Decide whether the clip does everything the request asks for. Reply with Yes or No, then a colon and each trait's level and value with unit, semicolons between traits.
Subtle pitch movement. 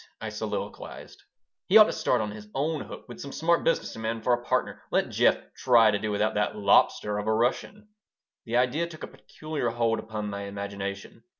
No: average, 5.1 semitones